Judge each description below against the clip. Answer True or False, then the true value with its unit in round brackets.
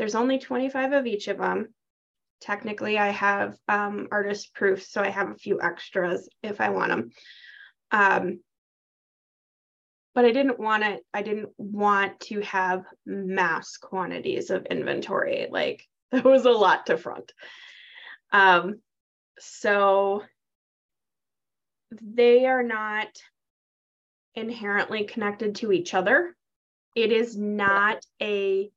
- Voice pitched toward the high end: True (210 Hz)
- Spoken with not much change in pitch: False (3.3 semitones)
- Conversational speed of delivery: False (125 wpm)